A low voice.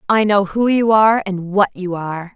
No: high, 200 Hz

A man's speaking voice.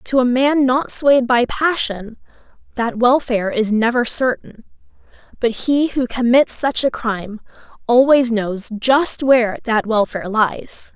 No: female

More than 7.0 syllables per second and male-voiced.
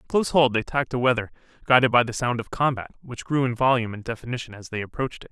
Yes: 7.4 syllables/s; male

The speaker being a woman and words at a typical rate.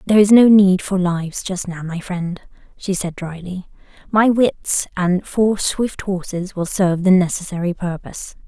Yes: female; average, 170 wpm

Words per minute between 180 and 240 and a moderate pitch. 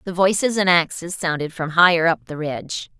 Yes: average, 200 wpm; medium, 170 Hz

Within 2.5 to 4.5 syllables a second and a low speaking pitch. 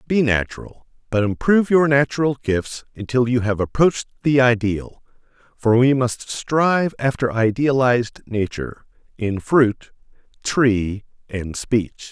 Yes: 4.4 syllables/s; low, 120 Hz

